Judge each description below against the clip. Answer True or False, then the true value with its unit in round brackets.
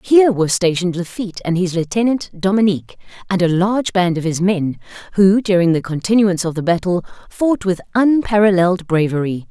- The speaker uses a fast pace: False (165 wpm)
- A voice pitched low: False (190 Hz)